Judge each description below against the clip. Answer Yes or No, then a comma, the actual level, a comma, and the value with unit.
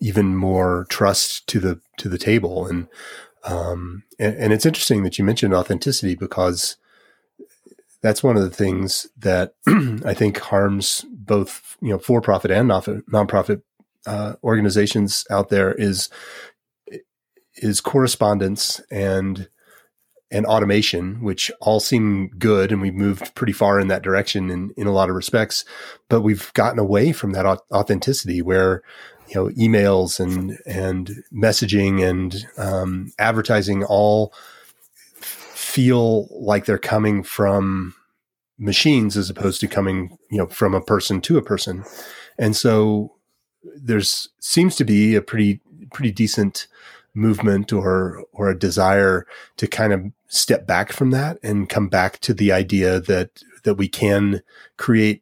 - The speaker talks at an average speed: Yes, average, 145 wpm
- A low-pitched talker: Yes, low, 100 Hz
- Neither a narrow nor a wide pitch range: No, narrow, 2.2 semitones